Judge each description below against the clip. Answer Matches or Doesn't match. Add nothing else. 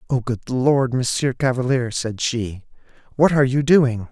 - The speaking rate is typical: Matches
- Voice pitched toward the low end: Matches